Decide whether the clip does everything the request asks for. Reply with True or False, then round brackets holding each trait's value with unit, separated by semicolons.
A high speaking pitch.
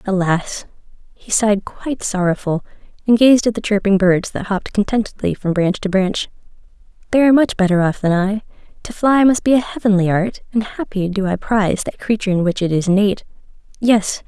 True (205 Hz)